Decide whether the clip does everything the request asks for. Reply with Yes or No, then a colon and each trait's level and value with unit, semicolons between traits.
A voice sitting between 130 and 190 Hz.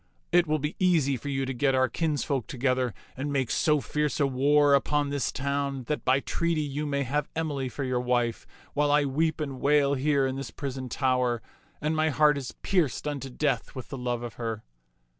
Yes: medium, 140 Hz